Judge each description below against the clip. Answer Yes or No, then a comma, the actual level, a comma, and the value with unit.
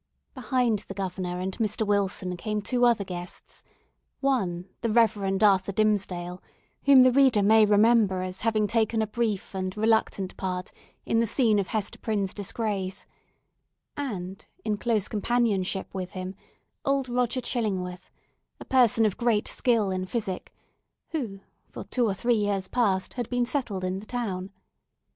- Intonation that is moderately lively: Yes, average, 3.7 semitones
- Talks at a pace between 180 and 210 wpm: No, average, 150 wpm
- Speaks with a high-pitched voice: Yes, high, 210 Hz